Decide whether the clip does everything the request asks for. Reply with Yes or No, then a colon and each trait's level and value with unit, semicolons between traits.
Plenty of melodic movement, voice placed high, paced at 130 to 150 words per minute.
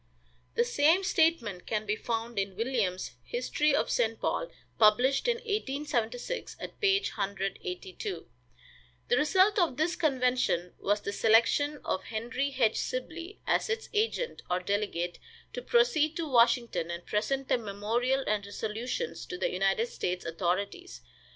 Yes: wide, 8.3 semitones; high, 245 Hz; average, 140 wpm